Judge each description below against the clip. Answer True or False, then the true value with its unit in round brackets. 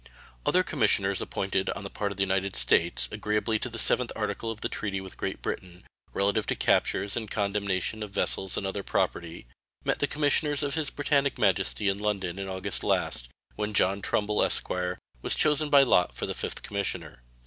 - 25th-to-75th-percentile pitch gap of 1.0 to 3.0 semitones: True (2.5 semitones)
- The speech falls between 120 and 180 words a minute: False (190 wpm)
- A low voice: True (100 Hz)